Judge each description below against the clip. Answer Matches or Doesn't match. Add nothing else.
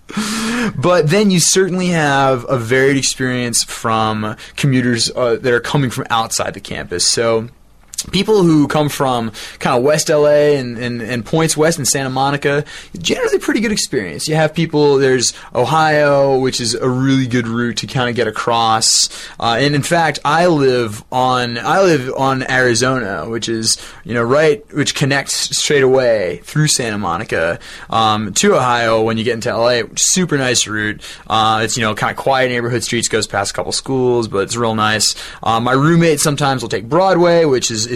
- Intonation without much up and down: Doesn't match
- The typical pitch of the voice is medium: Doesn't match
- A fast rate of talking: Doesn't match